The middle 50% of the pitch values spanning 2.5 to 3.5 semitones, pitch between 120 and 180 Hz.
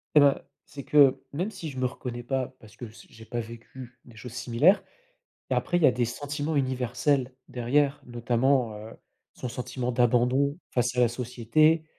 Yes: average, 2.8 semitones; low, 125 Hz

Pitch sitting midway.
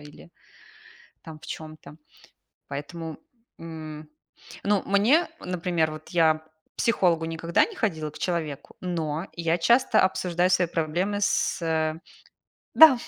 Yes: medium, 165 Hz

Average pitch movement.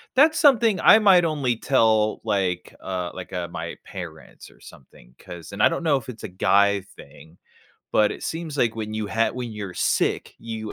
No: wide, 6.6 semitones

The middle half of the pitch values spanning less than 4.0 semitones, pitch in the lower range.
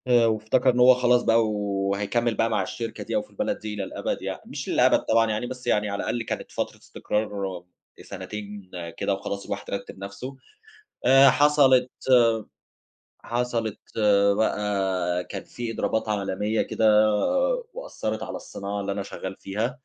Yes: average, 3.5 semitones; low, 110 Hz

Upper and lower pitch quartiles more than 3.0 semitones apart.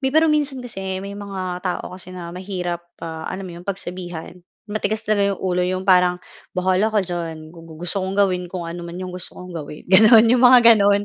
No: narrow, 2.5 semitones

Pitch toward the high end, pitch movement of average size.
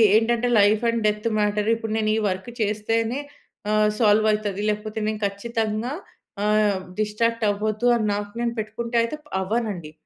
No: high, 215 Hz; narrow, 1.6 semitones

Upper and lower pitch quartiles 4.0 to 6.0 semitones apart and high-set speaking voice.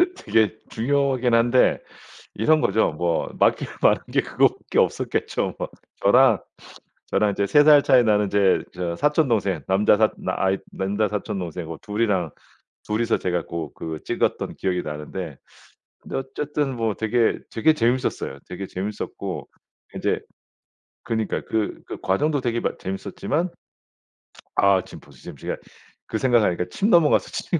No: average, 5.2 semitones; low, 110 Hz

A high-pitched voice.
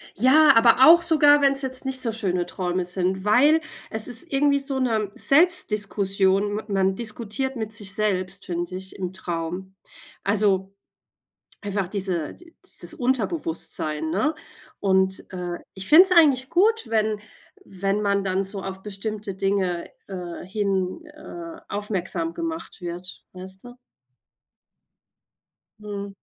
Yes: high, 205 Hz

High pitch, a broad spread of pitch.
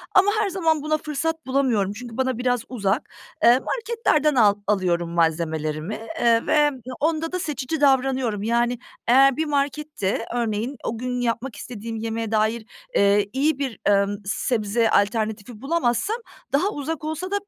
Yes: high, 245 Hz; wide, 5.7 semitones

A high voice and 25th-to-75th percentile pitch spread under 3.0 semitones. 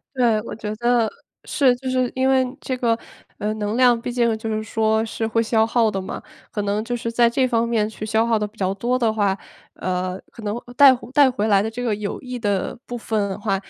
Yes: high, 225 Hz; narrow, 2.5 semitones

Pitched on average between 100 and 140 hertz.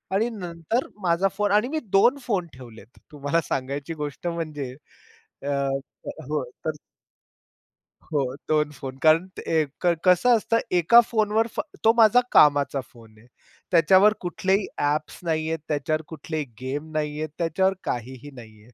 No: medium, 160 Hz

